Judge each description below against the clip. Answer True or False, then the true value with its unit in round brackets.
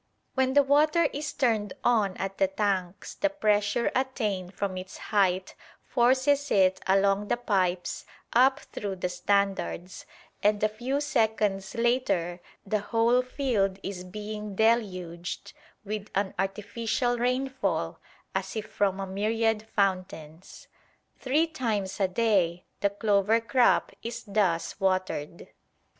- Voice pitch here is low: False (205 Hz)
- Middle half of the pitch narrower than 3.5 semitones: False (3.9 semitones)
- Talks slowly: True (125 wpm)